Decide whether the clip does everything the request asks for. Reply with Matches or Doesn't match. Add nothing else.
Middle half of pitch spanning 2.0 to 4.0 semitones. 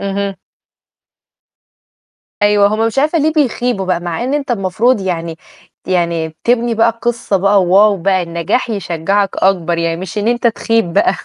Doesn't match